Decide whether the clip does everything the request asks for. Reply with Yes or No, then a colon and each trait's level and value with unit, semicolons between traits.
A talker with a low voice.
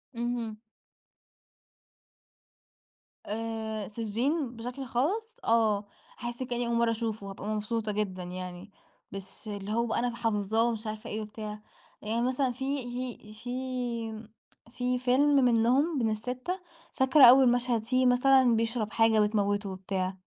No: high, 230 Hz